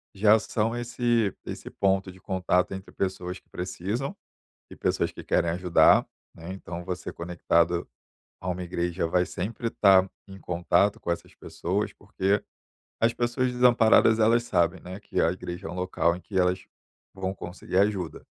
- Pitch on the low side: Yes, very low, 95 Hz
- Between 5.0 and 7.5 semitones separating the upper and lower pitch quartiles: No, average, 3.3 semitones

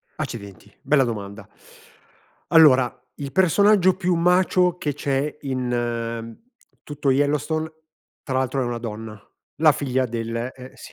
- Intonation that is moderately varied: Yes, average, 5.0 semitones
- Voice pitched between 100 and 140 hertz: Yes, low, 135 Hz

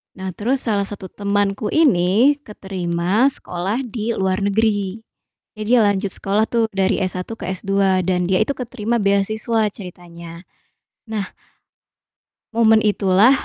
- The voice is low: No, high, 200 Hz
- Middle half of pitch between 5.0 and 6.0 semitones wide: No, average, 2.9 semitones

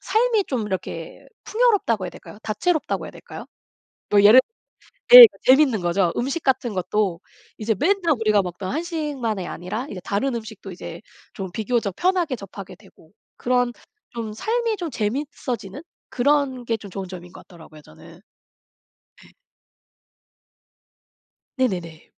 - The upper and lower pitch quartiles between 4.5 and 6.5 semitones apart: No, wide, 6.9 semitones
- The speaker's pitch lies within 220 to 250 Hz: Yes, high, 225 Hz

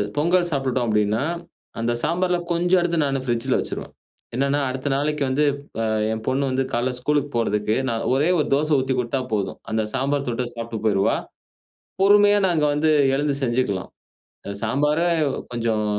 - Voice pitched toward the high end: No, low, 135 Hz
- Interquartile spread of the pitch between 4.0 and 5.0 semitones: Yes, average, 4.4 semitones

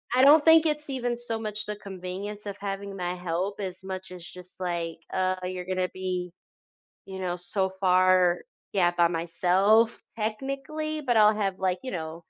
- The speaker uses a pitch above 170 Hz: Yes, high, 190 Hz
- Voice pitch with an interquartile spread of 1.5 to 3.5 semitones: Yes, average, 3.1 semitones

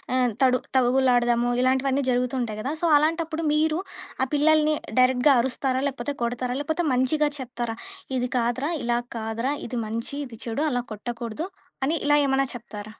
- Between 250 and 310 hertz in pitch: Yes, very high, 255 Hz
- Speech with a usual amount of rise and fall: Yes, average, 3.1 semitones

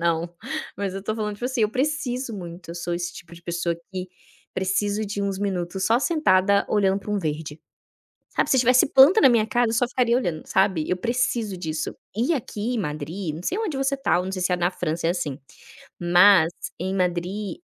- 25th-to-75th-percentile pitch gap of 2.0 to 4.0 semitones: No, average, 5.2 semitones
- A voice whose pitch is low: No, high, 195 Hz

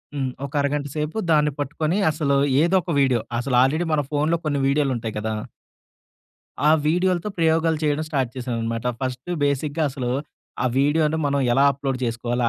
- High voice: No, medium, 145 Hz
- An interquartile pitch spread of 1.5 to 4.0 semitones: Yes, average, 3.4 semitones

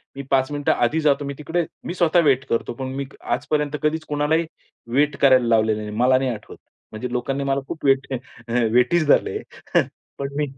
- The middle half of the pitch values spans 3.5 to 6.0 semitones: No, average, 2.9 semitones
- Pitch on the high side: No, medium, 140 Hz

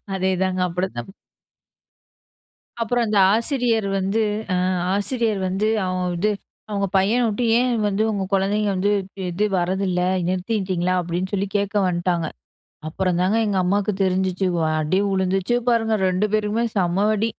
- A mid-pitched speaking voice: No, high, 195 Hz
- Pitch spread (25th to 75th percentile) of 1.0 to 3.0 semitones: Yes, narrow, 2.5 semitones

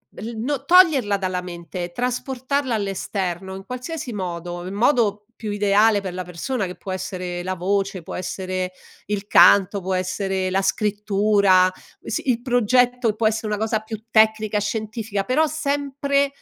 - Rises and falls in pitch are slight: No, average, 4.3 semitones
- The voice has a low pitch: No, high, 205 Hz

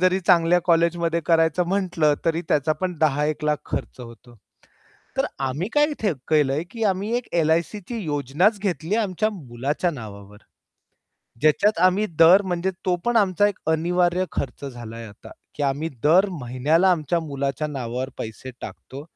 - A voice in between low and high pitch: Yes, medium, 165 Hz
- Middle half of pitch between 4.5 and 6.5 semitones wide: Yes, average, 4.8 semitones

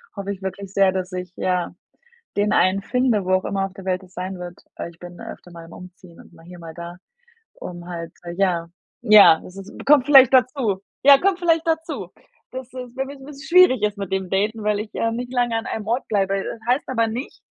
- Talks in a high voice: Yes, high, 200 Hz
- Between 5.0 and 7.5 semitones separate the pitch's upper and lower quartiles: Yes, wide, 5.5 semitones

